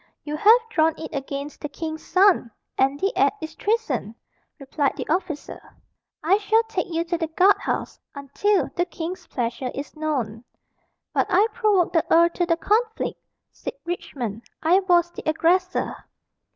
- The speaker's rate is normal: Yes, average, 160 wpm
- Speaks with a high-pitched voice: Yes, very high, 335 Hz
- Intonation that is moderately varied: Yes, average, 4.4 semitones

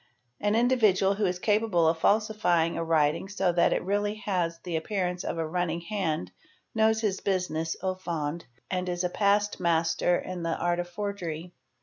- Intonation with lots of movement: No, average, 3.5 semitones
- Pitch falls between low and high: Yes, medium, 180 Hz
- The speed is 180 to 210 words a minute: Yes, average, 185 wpm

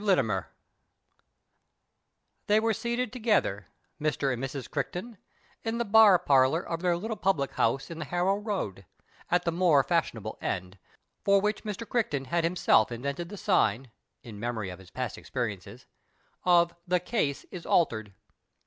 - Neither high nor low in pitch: Yes, medium, 170 Hz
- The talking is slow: No, average, 155 wpm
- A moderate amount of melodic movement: No, wide, 7.7 semitones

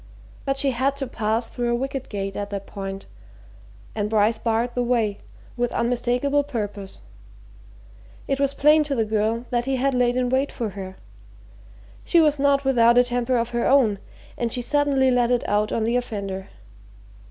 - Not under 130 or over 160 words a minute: No, average, 180 wpm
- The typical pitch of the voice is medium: No, high, 240 Hz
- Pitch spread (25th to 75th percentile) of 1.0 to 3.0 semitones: No, average, 3.6 semitones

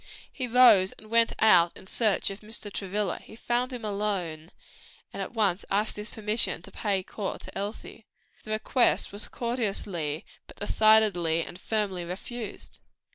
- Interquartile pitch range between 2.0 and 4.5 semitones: Yes, average, 2.8 semitones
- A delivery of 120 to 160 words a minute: Yes, average, 155 wpm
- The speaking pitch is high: Yes, high, 210 Hz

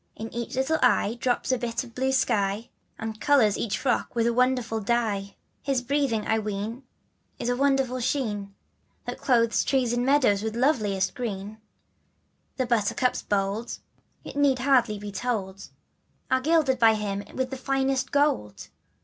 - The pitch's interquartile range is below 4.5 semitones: Yes, average, 3.7 semitones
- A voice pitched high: Yes, high, 240 Hz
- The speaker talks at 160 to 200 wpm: Yes, average, 165 wpm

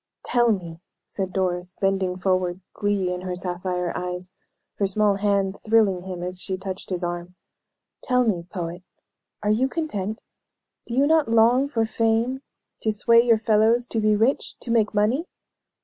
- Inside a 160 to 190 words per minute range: Yes, average, 165 wpm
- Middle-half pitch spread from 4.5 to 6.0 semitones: No, average, 3.8 semitones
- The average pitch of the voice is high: Yes, high, 200 Hz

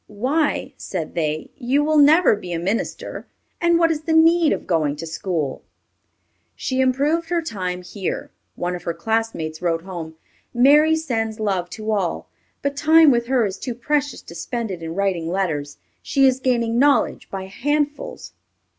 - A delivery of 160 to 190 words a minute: Yes, average, 170 wpm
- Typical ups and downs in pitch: No, wide, 8.5 semitones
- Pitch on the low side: No, high, 225 Hz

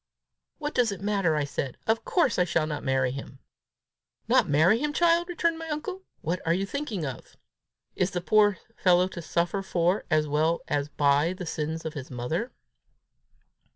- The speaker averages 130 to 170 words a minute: No, average, 180 wpm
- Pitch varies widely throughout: Yes, wide, 6.5 semitones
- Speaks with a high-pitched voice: No, medium, 175 Hz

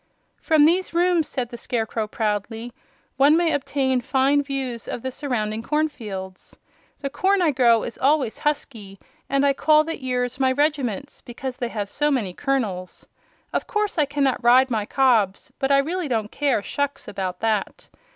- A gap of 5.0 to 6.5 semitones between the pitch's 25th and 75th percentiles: No, average, 4.3 semitones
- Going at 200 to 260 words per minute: No, average, 170 wpm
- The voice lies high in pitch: Yes, very high, 260 Hz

